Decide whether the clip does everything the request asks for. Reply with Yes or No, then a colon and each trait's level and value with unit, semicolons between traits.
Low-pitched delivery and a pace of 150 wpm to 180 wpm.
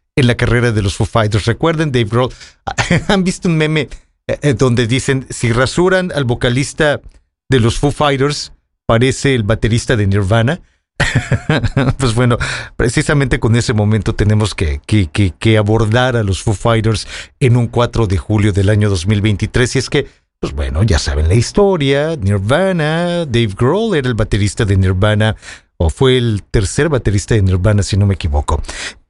Yes: low, 115 Hz; average, 165 wpm